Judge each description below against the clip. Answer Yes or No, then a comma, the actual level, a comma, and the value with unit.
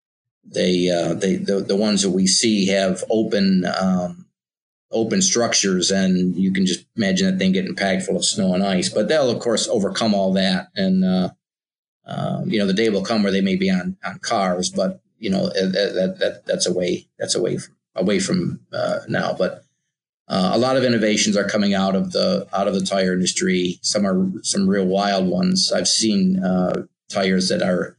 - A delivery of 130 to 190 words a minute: No, fast, 205 wpm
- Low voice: Yes, low, 100 Hz